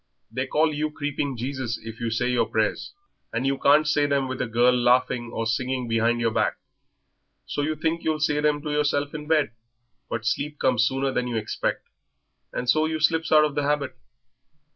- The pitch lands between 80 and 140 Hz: Yes, low, 135 Hz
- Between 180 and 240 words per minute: Yes, average, 200 wpm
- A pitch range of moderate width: Yes, average, 3.9 semitones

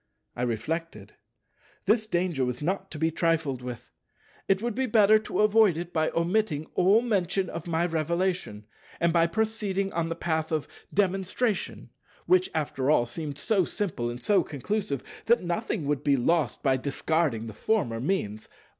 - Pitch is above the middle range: No, medium, 170 Hz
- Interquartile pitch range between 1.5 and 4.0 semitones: No, wide, 5.6 semitones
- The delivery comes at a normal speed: Yes, average, 160 wpm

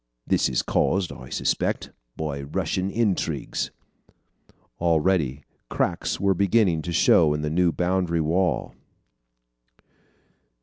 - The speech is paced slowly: Yes, slow, 105 wpm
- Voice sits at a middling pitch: No, very low, 85 Hz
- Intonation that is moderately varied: Yes, average, 3.7 semitones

